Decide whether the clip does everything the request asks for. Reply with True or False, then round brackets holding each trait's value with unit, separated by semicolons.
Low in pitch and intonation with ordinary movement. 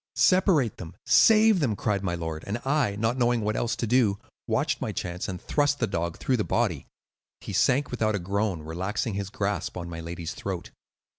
False (105 Hz; 5.8 semitones)